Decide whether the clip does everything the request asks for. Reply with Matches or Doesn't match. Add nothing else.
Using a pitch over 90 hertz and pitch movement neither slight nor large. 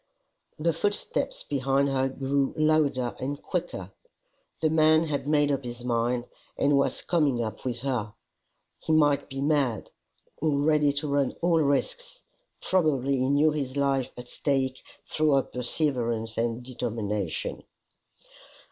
Matches